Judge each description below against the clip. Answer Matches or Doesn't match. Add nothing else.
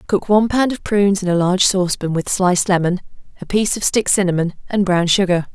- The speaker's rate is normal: Doesn't match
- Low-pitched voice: Doesn't match